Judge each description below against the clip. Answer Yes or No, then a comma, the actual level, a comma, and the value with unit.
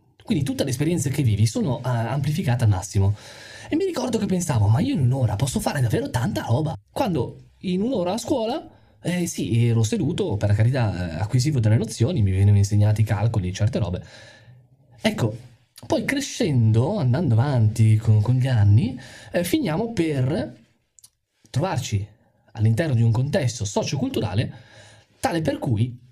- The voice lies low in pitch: Yes, low, 120 Hz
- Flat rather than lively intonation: No, average, 3.7 semitones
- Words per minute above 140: Yes, average, 155 wpm